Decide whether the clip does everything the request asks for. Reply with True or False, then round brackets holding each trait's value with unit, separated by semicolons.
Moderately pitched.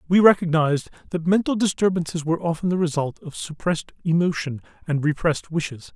True (165 Hz)